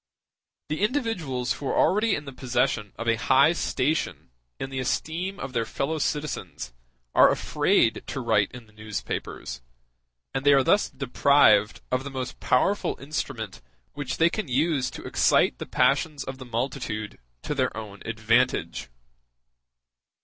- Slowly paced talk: No, average, 150 wpm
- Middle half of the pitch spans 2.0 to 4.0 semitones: No, average, 4.4 semitones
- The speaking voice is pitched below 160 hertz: Yes, low, 135 Hz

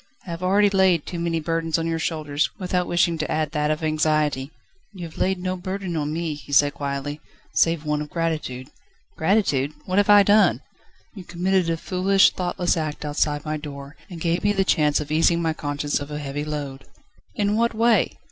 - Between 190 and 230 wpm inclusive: Yes, average, 200 wpm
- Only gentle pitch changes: No, average, 3.6 semitones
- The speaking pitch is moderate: Yes, medium, 165 Hz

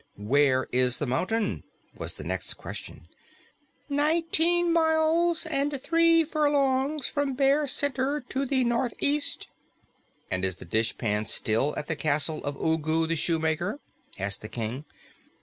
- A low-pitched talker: No, very high, 255 Hz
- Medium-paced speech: No, slow, 130 wpm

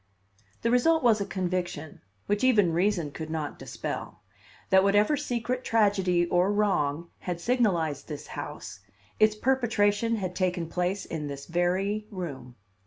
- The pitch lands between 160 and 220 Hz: Yes, high, 190 Hz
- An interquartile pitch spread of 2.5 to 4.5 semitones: Yes, average, 4.0 semitones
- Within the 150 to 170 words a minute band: No, average, 140 wpm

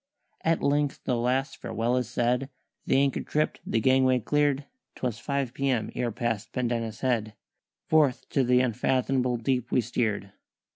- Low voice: Yes, low, 125 Hz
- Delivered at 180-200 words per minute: No, average, 150 wpm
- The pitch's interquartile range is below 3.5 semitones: Yes, narrow, 2.4 semitones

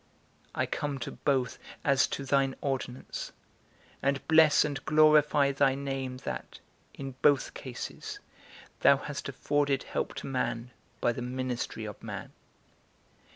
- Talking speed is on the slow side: Yes, slow, 130 wpm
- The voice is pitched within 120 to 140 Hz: Yes, low, 135 Hz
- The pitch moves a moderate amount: No, narrow, 1.8 semitones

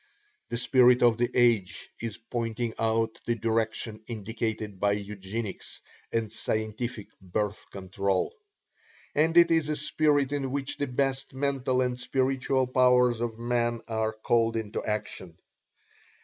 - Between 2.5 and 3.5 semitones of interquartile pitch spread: Yes, average, 2.9 semitones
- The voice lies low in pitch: Yes, low, 115 Hz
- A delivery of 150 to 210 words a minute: No, slow, 135 wpm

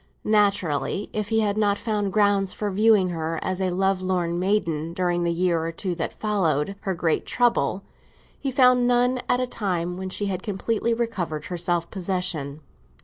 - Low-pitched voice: No, high, 190 Hz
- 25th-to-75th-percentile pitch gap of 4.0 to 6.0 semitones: No, average, 3.6 semitones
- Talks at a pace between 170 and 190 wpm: Yes, average, 175 wpm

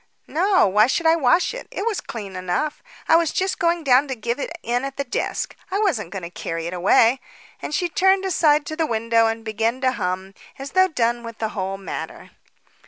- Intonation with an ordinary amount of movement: No, wide, 7.2 semitones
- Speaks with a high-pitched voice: Yes, high, 245 Hz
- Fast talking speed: Yes, fast, 220 wpm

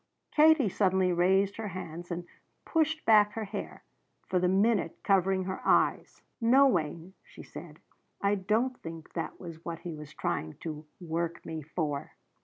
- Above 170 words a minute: No, average, 160 wpm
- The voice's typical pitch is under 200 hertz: Yes, medium, 185 Hz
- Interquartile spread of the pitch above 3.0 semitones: Yes, average, 4.2 semitones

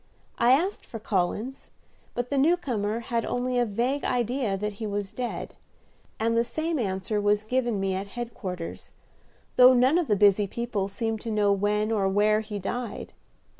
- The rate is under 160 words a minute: No, average, 175 wpm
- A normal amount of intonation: Yes, average, 3.3 semitones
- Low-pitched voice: No, high, 225 Hz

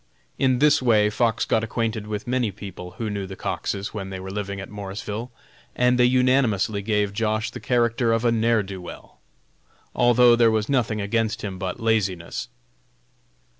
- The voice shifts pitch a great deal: No, average, 2.9 semitones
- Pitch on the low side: Yes, low, 110 Hz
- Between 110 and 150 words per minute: No, average, 175 wpm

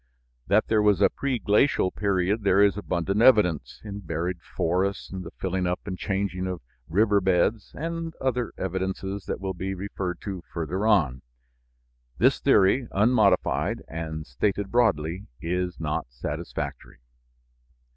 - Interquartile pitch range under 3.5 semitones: Yes, average, 2.7 semitones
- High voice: No, very low, 95 Hz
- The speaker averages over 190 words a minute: No, slow, 135 wpm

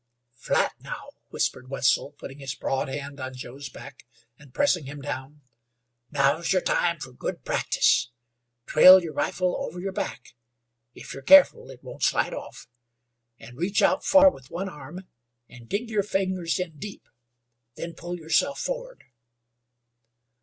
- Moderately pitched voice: Yes, medium, 155 Hz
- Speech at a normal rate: Yes, average, 150 wpm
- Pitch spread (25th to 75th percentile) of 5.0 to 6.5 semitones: Yes, wide, 5.6 semitones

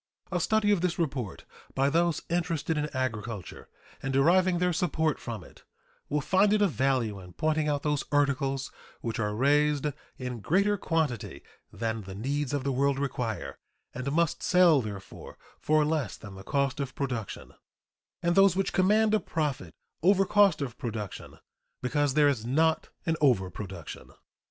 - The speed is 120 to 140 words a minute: No, average, 160 wpm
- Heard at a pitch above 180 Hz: No, medium, 145 Hz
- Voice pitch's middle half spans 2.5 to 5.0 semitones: No, wide, 5.4 semitones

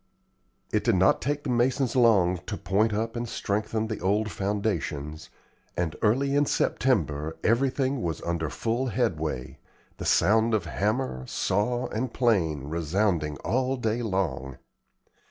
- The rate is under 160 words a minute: Yes, slow, 135 wpm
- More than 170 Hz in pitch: No, low, 105 Hz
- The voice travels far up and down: Yes, wide, 6.0 semitones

